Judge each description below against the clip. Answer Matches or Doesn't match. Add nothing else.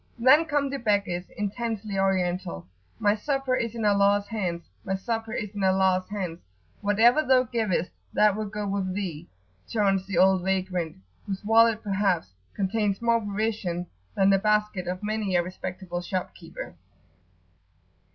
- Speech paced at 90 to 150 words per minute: Matches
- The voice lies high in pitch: Matches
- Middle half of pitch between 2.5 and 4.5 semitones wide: Matches